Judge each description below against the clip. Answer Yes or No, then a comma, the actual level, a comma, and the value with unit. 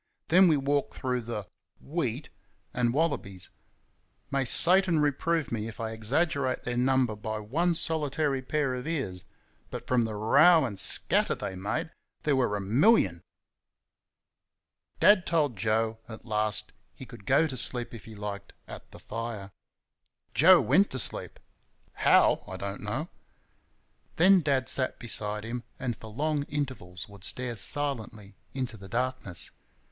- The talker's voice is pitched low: Yes, low, 125 Hz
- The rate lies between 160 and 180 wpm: No, average, 150 wpm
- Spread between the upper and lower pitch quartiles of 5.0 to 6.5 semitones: Yes, wide, 5.4 semitones